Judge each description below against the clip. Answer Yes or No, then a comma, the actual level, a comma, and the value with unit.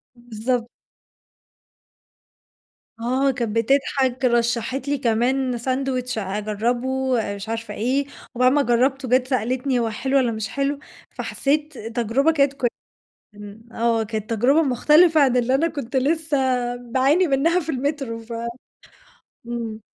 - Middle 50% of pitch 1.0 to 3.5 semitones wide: Yes, average, 3.1 semitones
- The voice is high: Yes, very high, 255 Hz